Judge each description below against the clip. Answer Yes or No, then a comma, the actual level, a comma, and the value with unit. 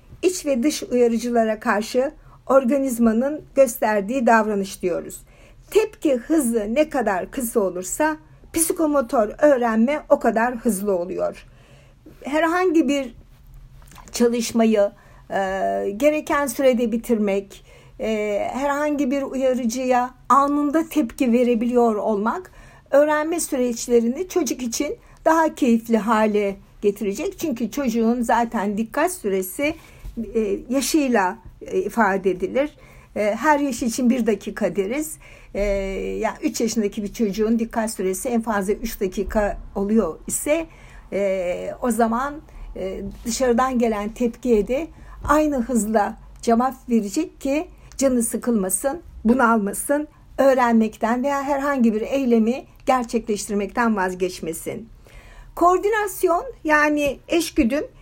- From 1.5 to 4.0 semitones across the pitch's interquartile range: No, average, 4.9 semitones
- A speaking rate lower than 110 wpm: Yes, average, 100 wpm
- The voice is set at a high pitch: Yes, high, 240 Hz